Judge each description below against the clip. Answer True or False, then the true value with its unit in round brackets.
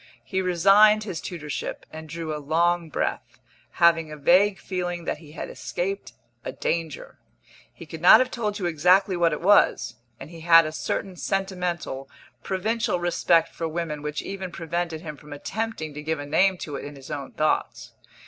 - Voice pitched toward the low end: False (170 Hz)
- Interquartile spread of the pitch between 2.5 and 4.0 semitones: True (3.4 semitones)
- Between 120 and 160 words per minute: False (180 wpm)